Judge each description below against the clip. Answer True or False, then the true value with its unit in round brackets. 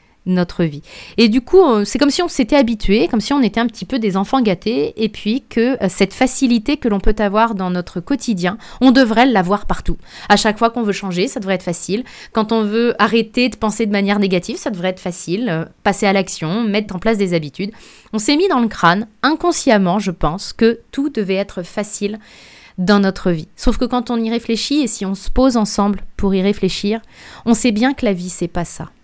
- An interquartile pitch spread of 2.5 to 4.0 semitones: True (3.7 semitones)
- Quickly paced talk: True (225 wpm)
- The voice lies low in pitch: False (215 Hz)